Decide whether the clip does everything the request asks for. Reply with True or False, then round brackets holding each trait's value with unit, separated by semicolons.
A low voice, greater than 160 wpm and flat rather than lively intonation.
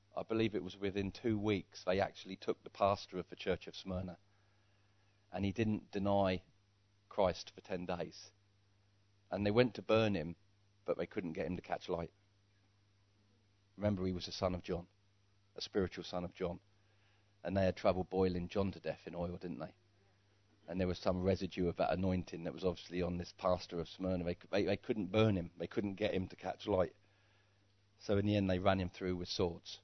True (100 Hz; 205 wpm; 1.7 semitones)